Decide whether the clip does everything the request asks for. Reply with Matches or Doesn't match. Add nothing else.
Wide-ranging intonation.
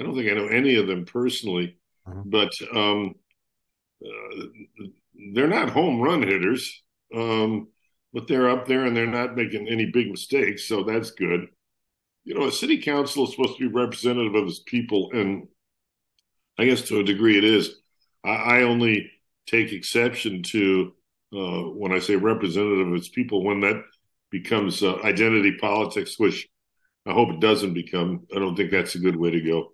Doesn't match